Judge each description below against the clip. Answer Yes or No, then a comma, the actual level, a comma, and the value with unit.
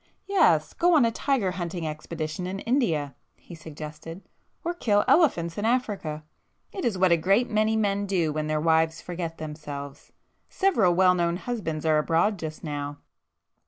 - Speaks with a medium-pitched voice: Yes, medium, 175 Hz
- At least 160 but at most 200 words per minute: No, average, 150 wpm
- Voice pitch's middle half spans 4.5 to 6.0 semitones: Yes, wide, 5.4 semitones